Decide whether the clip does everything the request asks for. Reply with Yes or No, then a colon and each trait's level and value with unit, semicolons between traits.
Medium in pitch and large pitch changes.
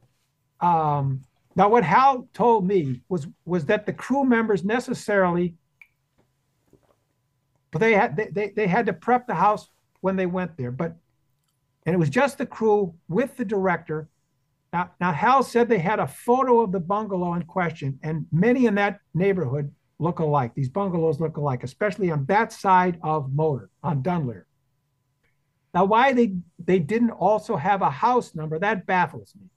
Yes: medium, 175 Hz; wide, 6.5 semitones